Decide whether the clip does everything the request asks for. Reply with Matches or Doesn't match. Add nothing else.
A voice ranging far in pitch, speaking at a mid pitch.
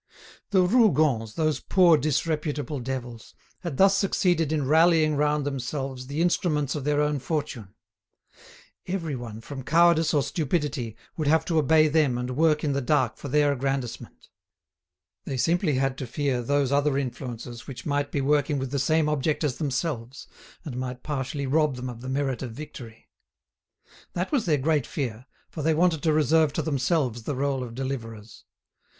Doesn't match